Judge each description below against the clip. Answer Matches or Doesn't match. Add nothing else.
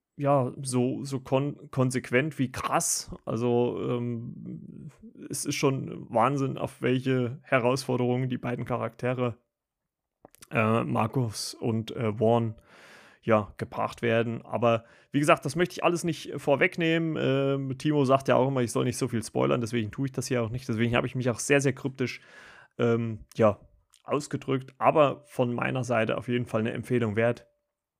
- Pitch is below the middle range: Matches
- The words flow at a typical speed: Matches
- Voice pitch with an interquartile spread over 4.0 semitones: Doesn't match